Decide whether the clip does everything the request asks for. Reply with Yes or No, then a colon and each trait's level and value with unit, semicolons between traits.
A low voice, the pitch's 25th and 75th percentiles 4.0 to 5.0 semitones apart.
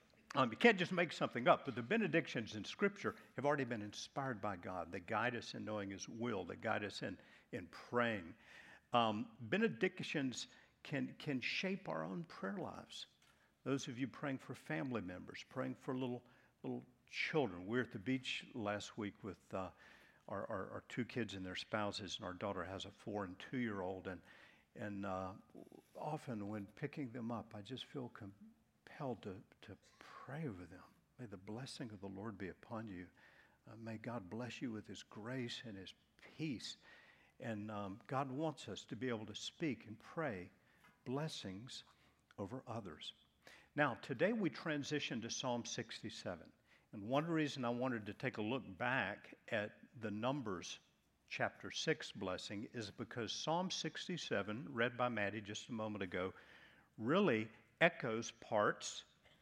Yes: low, 115 Hz; average, 4.5 semitones